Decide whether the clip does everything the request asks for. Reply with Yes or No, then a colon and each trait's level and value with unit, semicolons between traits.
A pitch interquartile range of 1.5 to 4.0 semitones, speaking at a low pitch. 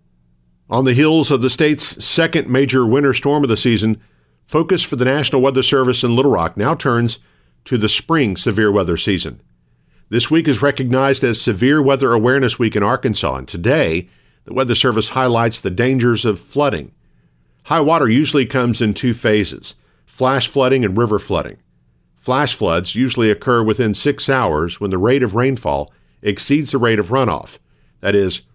No: average, 5.2 semitones; low, 120 Hz